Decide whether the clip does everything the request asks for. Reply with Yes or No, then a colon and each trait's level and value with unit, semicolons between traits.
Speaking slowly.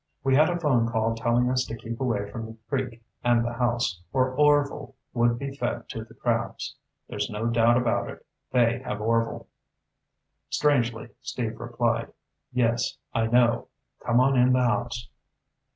No: average, 165 wpm